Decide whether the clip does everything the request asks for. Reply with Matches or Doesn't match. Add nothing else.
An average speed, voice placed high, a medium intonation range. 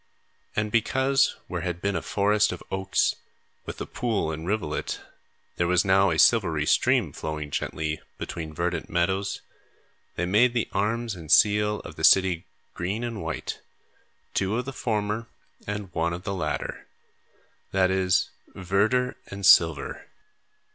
Doesn't match